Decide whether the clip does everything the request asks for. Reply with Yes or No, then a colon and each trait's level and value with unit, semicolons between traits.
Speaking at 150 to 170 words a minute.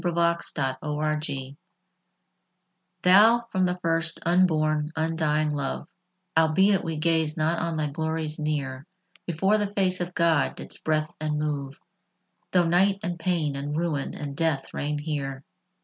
No: average, 140 wpm